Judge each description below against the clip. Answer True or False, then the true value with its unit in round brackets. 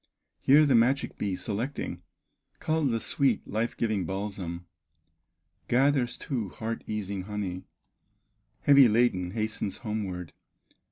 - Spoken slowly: True (110 wpm)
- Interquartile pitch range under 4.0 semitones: False (4.3 semitones)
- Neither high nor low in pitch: False (110 Hz)